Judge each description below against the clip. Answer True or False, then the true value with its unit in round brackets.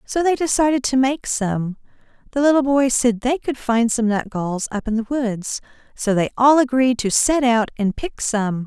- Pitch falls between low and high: False (240 Hz)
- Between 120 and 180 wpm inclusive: False (200 wpm)